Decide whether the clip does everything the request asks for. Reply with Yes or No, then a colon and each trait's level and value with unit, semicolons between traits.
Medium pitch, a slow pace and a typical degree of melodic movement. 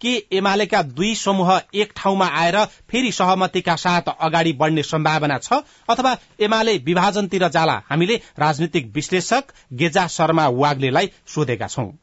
Yes: medium, 180 Hz; slow, 130 wpm; average, 4.3 semitones